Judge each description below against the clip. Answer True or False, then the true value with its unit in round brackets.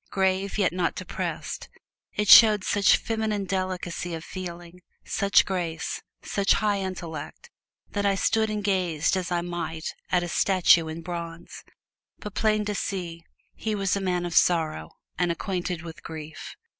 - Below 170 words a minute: True (155 wpm)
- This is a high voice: False (180 Hz)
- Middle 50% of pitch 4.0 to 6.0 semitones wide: False (2.9 semitones)